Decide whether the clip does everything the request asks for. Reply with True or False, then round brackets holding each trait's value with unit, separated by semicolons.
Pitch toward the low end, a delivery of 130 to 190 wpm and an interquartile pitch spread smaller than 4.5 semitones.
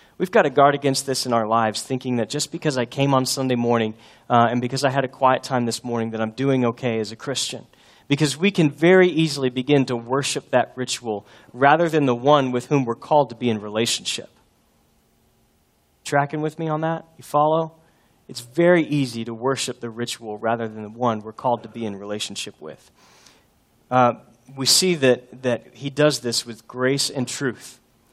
False (125 Hz; 200 wpm; 3.4 semitones)